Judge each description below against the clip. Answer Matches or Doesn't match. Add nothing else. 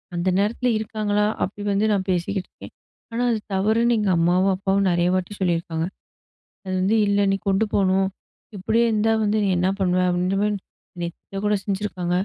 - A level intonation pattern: Matches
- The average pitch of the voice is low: Doesn't match